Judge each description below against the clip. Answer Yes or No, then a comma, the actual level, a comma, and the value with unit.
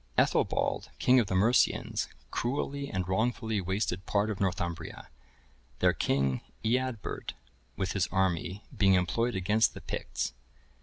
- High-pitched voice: No, low, 100 Hz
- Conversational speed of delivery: No, slow, 125 wpm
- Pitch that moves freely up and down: No, average, 3.9 semitones